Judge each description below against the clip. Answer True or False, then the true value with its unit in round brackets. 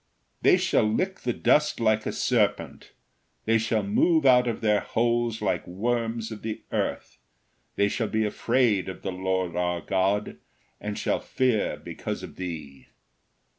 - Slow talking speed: False (155 wpm)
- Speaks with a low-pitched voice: True (110 Hz)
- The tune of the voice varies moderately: True (3.7 semitones)